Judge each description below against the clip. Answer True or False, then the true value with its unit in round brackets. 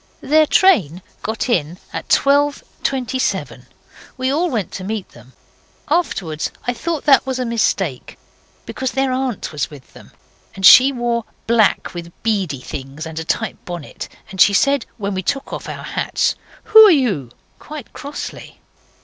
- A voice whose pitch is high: True (230 Hz)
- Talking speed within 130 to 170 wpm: True (160 wpm)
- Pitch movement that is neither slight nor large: False (7.7 semitones)